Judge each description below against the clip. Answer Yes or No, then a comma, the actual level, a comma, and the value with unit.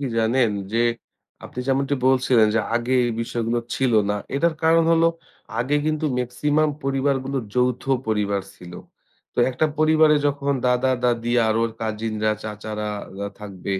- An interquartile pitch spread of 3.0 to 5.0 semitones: Yes, average, 3.9 semitones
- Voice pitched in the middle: No, low, 125 Hz